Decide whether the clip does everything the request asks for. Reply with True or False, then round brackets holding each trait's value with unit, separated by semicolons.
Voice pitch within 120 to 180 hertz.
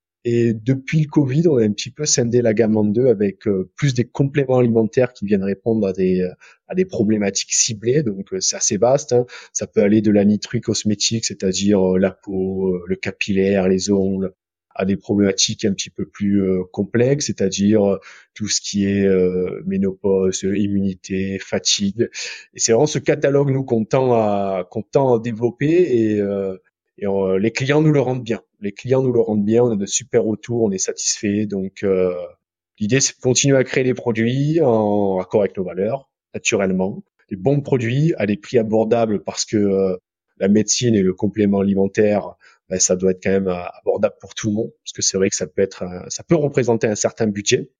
False (105 Hz)